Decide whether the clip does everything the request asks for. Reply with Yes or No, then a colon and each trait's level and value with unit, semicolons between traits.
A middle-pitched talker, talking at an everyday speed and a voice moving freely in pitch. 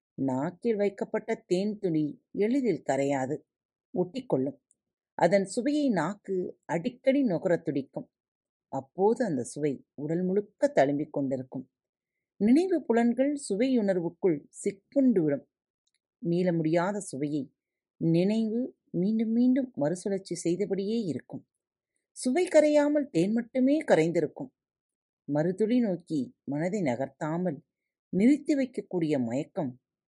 No: high, 195 Hz; average, 90 wpm; wide, 7.3 semitones